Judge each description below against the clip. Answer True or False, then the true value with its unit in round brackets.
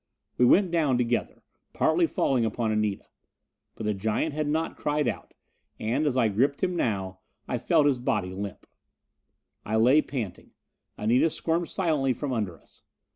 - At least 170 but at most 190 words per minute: False (160 wpm)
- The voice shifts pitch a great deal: True (5.9 semitones)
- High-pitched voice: False (125 Hz)